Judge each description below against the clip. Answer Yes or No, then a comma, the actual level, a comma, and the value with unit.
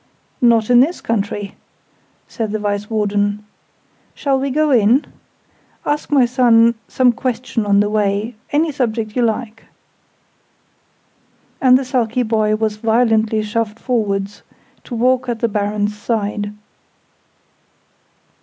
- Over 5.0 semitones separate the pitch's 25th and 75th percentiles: No, average, 3.0 semitones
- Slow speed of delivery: Yes, slow, 125 wpm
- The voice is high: Yes, high, 225 Hz